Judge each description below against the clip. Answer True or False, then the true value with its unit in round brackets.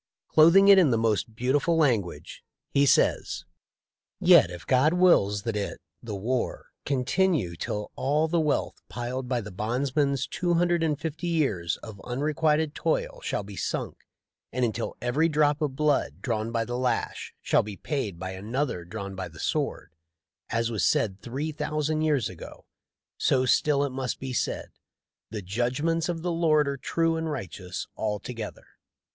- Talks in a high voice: False (130 Hz)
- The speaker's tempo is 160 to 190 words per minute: True (165 wpm)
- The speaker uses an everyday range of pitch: False (6.2 semitones)